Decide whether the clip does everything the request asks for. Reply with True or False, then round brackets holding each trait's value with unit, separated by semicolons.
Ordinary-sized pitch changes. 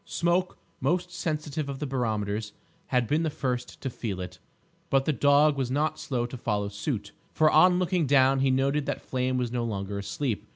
True (4.3 semitones)